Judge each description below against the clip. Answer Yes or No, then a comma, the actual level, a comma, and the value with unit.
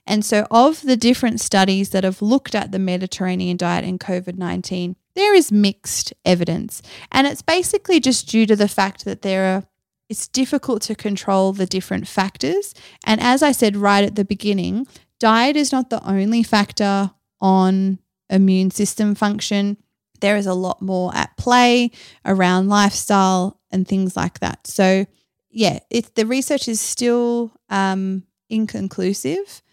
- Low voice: No, high, 205 Hz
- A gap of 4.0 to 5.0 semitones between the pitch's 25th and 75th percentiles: No, average, 3.6 semitones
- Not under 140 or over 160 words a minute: Yes, average, 155 wpm